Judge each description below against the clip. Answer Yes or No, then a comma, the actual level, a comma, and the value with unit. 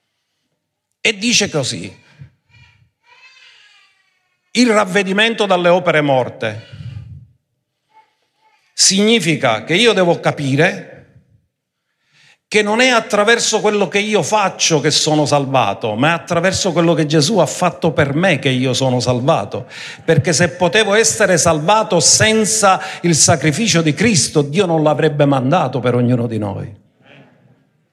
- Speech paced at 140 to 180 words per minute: No, average, 120 wpm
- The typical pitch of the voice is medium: Yes, medium, 170 Hz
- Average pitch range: No, wide, 7.0 semitones